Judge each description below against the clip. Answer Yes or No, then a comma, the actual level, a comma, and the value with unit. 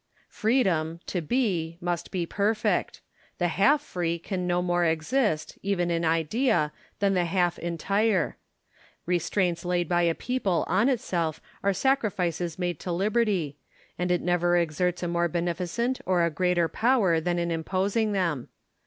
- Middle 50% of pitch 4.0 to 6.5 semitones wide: No, average, 2.9 semitones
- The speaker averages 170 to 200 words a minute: No, average, 150 wpm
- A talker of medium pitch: Yes, medium, 175 Hz